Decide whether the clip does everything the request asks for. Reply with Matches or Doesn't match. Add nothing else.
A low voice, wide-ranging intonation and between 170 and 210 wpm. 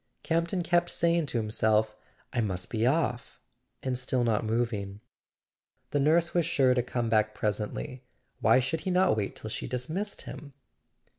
Doesn't match